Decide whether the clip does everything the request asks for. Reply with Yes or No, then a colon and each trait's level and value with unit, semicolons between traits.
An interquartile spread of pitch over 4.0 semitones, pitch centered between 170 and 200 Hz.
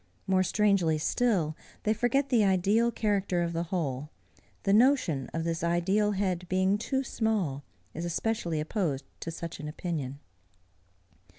Yes: average, 4.4 semitones; medium, 185 Hz